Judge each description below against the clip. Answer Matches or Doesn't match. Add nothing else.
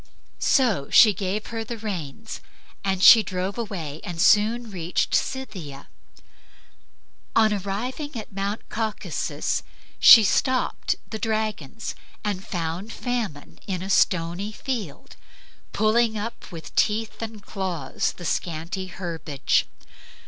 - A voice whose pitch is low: Doesn't match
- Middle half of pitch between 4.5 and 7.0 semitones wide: Doesn't match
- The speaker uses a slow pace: Matches